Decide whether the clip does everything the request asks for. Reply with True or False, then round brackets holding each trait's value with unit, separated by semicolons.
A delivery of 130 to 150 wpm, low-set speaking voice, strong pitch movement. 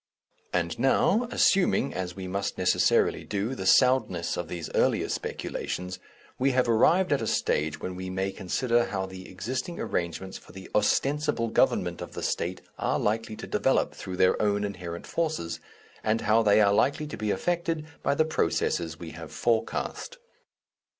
False (165 wpm; 105 Hz; 6.5 semitones)